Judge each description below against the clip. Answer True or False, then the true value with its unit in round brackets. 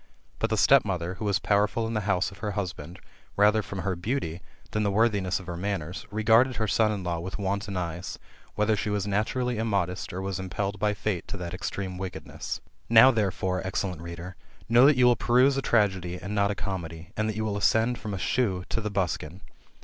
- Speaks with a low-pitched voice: True (100 Hz)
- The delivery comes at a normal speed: False (210 wpm)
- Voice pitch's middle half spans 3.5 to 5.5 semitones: False (2.9 semitones)